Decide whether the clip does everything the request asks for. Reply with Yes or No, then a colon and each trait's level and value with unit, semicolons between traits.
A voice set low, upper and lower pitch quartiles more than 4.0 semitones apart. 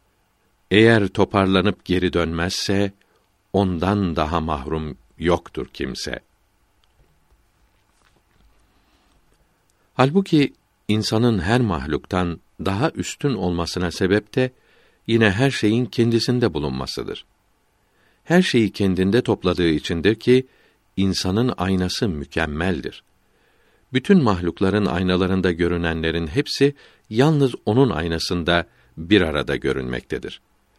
Yes: very low, 95 Hz; average, 4.7 semitones